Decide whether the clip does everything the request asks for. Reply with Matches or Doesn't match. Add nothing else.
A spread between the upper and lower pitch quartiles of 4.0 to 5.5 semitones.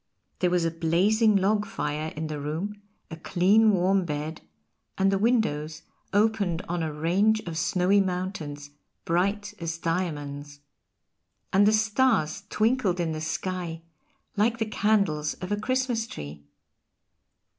Matches